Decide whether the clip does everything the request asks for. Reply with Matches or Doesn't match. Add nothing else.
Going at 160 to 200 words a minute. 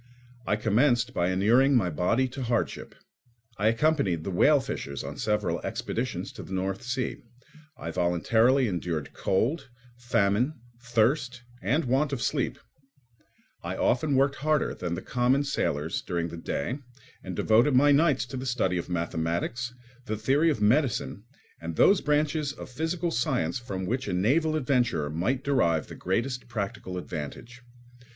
Doesn't match